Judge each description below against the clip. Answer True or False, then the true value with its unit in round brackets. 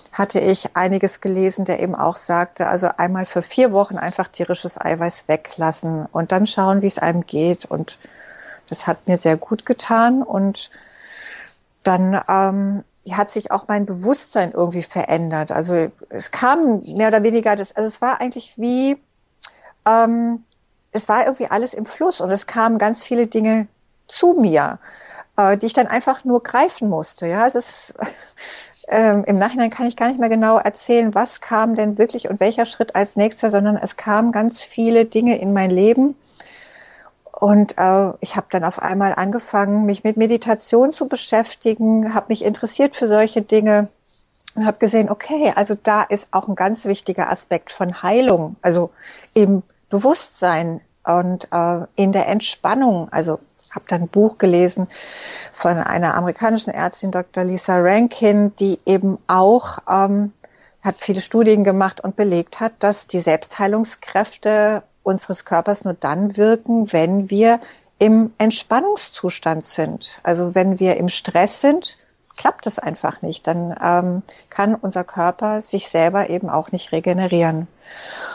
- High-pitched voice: True (200 Hz)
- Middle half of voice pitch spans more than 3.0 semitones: True (3.6 semitones)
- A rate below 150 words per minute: False (155 wpm)